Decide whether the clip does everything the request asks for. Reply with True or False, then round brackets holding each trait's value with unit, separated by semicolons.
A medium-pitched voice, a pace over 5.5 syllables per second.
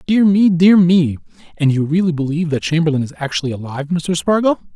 True (165 Hz; 6.4 syllables/s)